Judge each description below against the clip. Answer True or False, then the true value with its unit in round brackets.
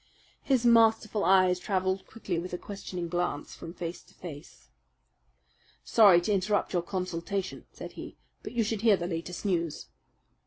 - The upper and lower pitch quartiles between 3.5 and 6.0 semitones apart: False (3.1 semitones)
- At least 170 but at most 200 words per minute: False (155 wpm)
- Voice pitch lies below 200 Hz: True (185 Hz)